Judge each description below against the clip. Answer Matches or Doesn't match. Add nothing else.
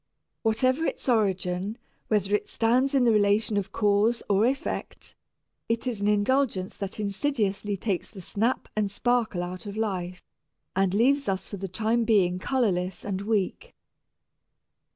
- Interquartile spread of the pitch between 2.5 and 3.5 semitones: Matches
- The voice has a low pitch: Doesn't match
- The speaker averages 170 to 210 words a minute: Doesn't match